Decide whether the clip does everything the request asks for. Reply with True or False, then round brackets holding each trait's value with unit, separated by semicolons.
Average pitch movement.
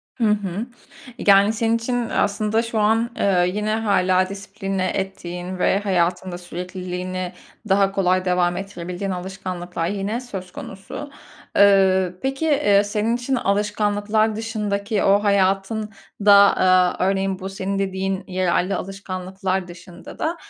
False (2.2 semitones)